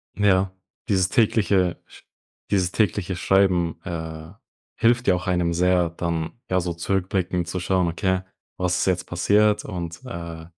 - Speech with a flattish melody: Yes, narrow, 2.1 semitones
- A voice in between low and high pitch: No, very low, 90 Hz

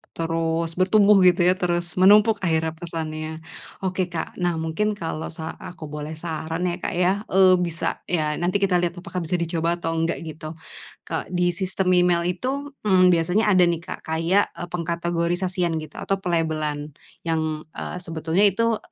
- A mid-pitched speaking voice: Yes, medium, 175 Hz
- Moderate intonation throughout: No, narrow, 2.1 semitones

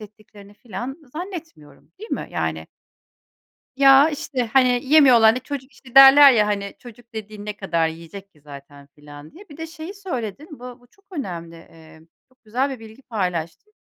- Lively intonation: Yes, wide, 6.3 semitones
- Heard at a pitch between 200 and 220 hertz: No, high, 235 Hz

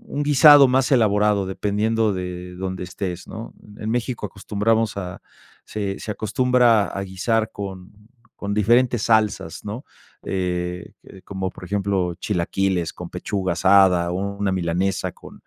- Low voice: Yes, low, 100 Hz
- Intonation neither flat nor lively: Yes, average, 3.1 semitones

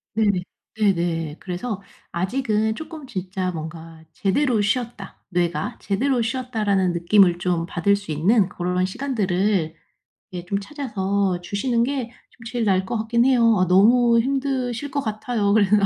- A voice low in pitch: No, high, 205 Hz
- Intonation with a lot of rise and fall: No, average, 4.8 semitones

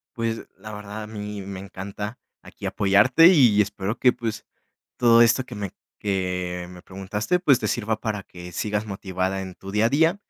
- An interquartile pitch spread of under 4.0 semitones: Yes, average, 3.1 semitones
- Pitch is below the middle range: Yes, low, 105 Hz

